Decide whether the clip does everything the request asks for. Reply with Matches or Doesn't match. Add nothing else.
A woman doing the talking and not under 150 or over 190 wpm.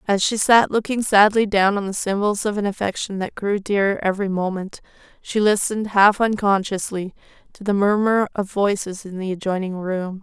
Matches